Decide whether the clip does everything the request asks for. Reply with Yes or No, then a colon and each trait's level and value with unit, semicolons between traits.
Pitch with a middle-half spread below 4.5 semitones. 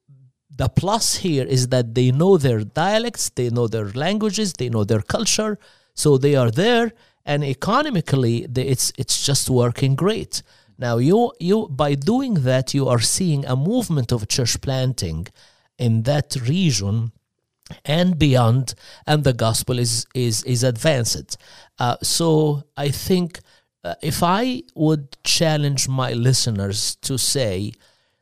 No: average, 5.1 semitones